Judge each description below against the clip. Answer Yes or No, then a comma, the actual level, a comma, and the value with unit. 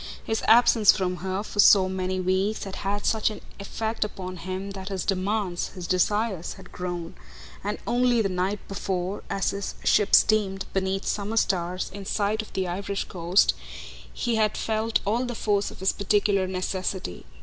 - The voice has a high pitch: Yes, high, 195 Hz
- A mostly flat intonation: Yes, narrow, 2.2 semitones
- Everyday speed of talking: Yes, average, 170 wpm